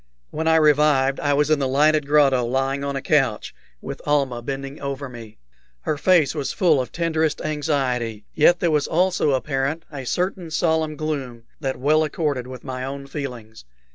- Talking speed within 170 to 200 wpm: Yes, average, 175 wpm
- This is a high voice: No, medium, 140 Hz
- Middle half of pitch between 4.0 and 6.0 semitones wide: No, average, 2.7 semitones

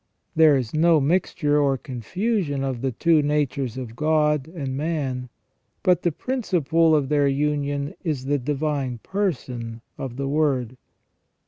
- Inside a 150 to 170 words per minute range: No, average, 140 wpm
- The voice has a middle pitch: Yes, medium, 145 Hz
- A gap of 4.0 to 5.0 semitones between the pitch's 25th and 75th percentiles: No, average, 3.1 semitones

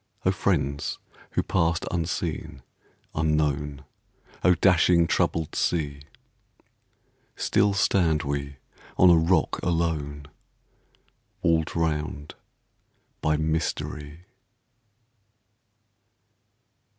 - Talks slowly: Yes, slow, 75 wpm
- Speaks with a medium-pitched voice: No, very low, 80 Hz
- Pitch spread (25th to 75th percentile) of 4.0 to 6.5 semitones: No, narrow, 2.4 semitones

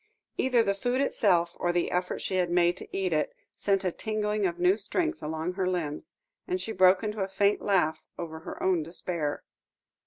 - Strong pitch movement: No, average, 3.3 semitones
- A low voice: No, medium, 185 Hz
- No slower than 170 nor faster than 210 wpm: Yes, average, 195 wpm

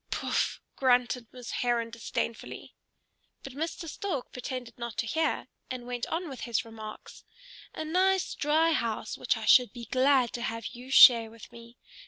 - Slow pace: No, average, 165 wpm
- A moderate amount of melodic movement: Yes, average, 3.6 semitones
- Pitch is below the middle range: No, high, 245 Hz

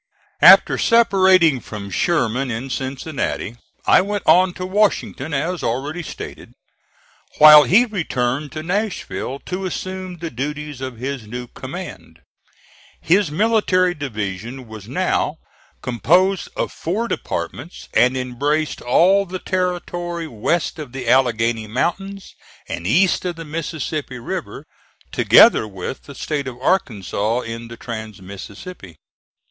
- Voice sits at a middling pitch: Yes, medium, 150 Hz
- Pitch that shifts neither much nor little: No, wide, 6.9 semitones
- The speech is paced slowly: Yes, slow, 125 wpm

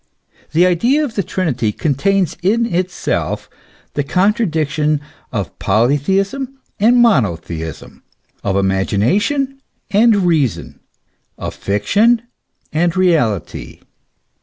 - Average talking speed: No, slow, 90 wpm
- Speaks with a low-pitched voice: No, medium, 175 Hz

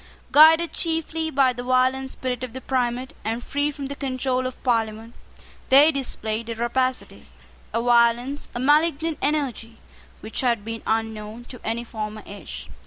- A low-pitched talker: No, very high, 255 Hz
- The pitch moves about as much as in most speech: Yes, average, 3.3 semitones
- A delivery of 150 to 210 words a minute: Yes, average, 155 wpm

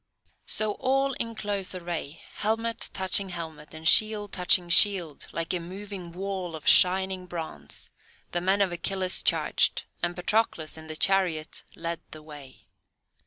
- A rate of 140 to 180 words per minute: Yes, average, 145 wpm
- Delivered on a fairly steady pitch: No, average, 3.2 semitones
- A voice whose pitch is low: No, medium, 180 Hz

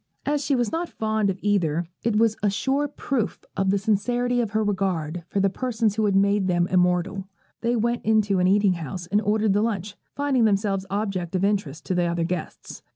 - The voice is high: Yes, high, 205 Hz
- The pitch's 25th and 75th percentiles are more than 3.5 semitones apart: No, average, 3.0 semitones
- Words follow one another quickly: Yes, fast, 210 wpm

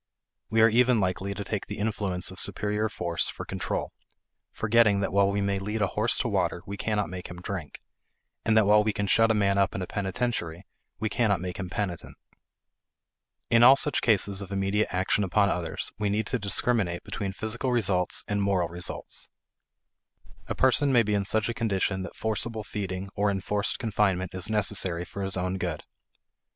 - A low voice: Yes, low, 100 Hz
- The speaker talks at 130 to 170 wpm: No, average, 190 wpm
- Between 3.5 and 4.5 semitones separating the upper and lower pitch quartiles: No, narrow, 2.5 semitones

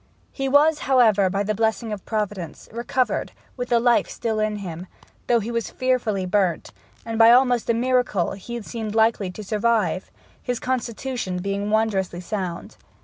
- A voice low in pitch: No, high, 220 Hz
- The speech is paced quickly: No, average, 160 wpm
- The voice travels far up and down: No, average, 3.3 semitones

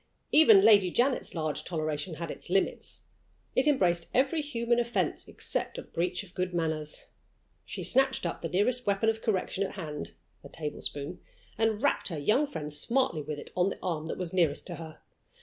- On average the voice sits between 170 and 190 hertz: Yes, medium, 185 Hz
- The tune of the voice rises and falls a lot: Yes, wide, 6.8 semitones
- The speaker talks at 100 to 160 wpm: No, average, 185 wpm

